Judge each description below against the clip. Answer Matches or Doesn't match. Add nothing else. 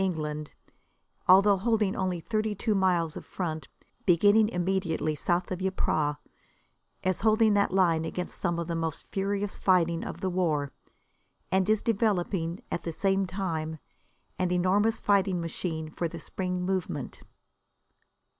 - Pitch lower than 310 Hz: Matches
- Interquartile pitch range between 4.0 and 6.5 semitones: Doesn't match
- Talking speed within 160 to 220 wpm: Doesn't match